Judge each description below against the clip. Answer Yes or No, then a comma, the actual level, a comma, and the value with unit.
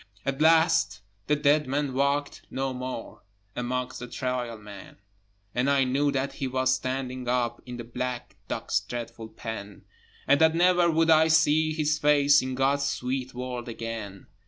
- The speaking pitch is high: No, low, 130 Hz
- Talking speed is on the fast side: No, average, 160 wpm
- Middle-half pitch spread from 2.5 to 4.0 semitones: Yes, average, 2.9 semitones